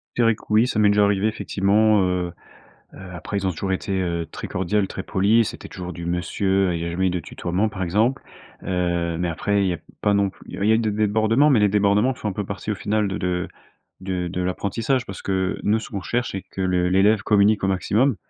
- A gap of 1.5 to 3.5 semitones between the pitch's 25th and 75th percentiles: Yes, average, 2.7 semitones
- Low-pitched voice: Yes, low, 100 Hz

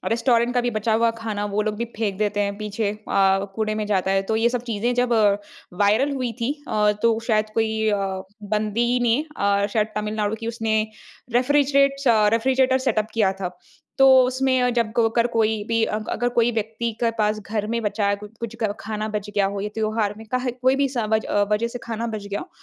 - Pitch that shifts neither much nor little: No, narrow, 2.2 semitones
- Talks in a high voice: Yes, high, 220 Hz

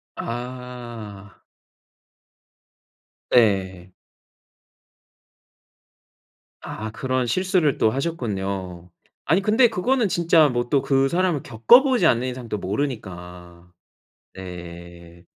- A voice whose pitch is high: No, low, 120 Hz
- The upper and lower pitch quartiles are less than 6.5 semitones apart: No, wide, 7.8 semitones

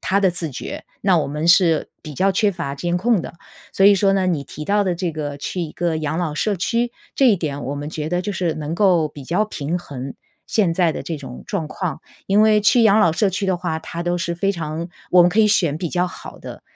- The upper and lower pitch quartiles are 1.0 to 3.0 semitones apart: No, average, 4.0 semitones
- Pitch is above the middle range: No, medium, 175 Hz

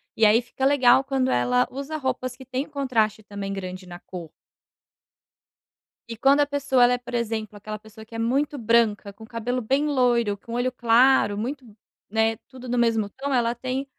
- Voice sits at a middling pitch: No, high, 240 Hz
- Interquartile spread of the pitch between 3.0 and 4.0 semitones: Yes, average, 3.4 semitones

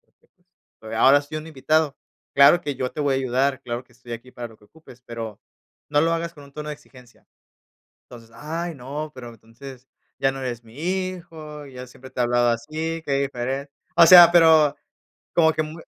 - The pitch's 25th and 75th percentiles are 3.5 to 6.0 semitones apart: Yes, average, 4.2 semitones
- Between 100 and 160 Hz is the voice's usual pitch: Yes, medium, 140 Hz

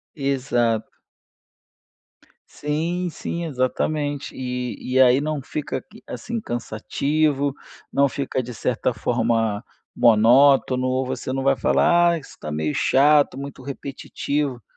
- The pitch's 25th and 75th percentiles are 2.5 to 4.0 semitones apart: Yes, average, 2.9 semitones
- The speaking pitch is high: No, low, 135 Hz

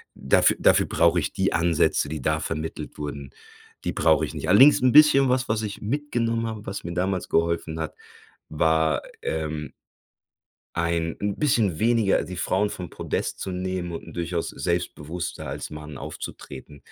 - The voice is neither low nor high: No, very low, 85 Hz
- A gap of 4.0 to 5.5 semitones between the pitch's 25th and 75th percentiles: Yes, average, 4.7 semitones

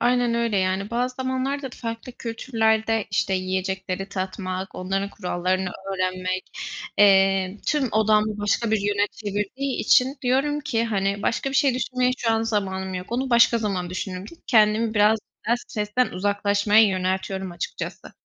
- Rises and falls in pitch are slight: No, average, 3.6 semitones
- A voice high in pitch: Yes, high, 210 Hz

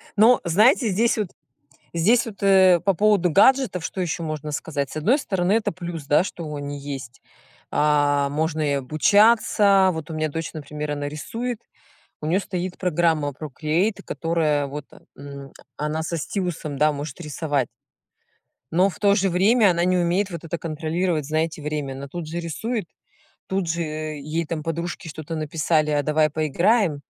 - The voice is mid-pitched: Yes, medium, 165 Hz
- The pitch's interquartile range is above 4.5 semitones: No, average, 3.8 semitones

